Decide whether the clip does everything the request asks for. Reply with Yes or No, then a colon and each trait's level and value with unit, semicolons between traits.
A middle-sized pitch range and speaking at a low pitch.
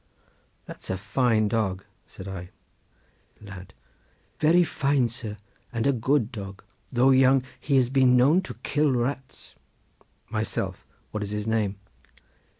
Yes: average, 4.5 semitones; low, 120 Hz